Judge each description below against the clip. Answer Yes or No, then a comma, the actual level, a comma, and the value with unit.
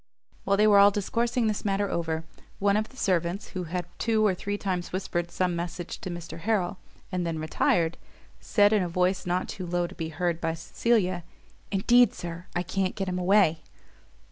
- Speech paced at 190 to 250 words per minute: Yes, average, 195 wpm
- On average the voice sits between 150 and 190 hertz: Yes, medium, 185 Hz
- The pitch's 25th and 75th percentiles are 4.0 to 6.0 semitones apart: No, average, 2.8 semitones